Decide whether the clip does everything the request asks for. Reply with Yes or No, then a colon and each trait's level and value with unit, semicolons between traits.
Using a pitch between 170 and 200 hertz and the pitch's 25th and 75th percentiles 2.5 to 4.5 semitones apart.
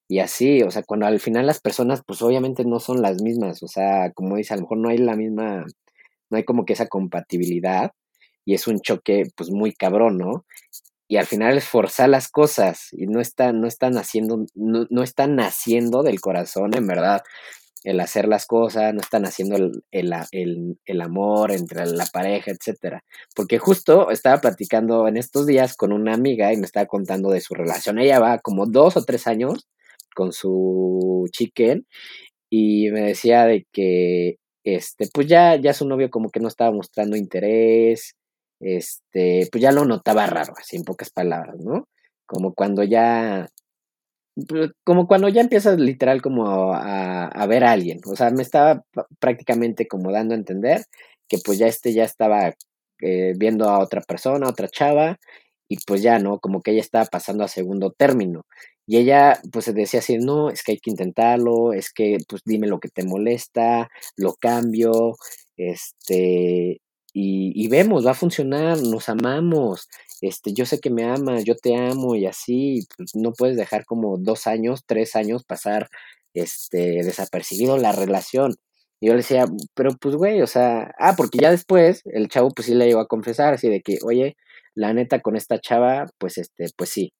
No: low, 115 Hz; average, 4.1 semitones